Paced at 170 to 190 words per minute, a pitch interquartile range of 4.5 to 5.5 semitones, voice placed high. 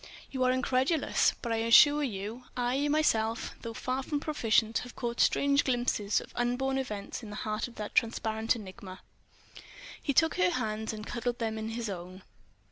No: average, 175 wpm; average, 3.1 semitones; high, 235 Hz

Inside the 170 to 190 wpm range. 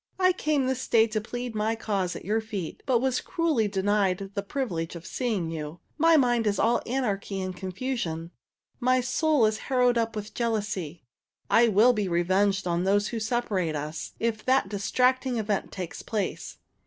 Yes: average, 175 wpm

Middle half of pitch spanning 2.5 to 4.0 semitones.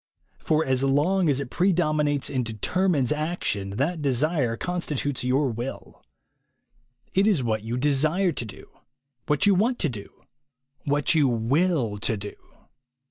No: wide, 5.6 semitones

